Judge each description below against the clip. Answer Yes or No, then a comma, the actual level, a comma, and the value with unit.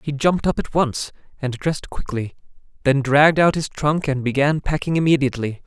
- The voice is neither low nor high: Yes, medium, 145 Hz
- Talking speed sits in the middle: Yes, average, 180 wpm